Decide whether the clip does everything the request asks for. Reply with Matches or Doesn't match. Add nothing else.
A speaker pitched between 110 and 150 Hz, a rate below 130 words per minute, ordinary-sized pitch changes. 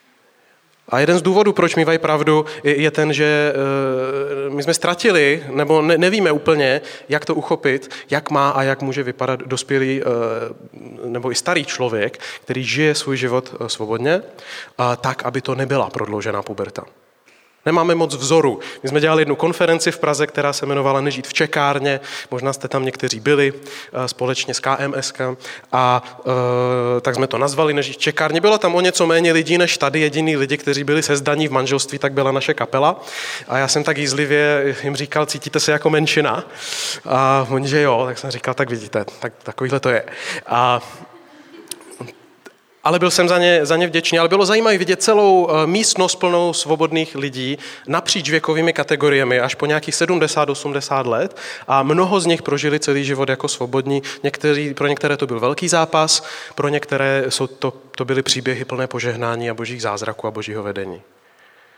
Doesn't match